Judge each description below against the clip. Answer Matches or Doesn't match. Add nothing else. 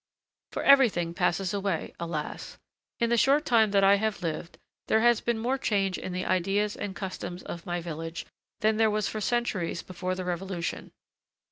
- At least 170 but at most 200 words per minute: Matches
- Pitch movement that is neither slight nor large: Matches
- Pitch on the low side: Doesn't match